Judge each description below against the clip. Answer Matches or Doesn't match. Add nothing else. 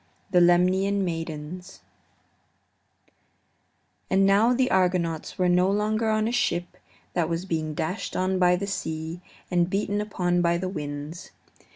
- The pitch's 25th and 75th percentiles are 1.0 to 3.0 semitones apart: Matches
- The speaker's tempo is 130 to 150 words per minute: Matches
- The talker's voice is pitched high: Doesn't match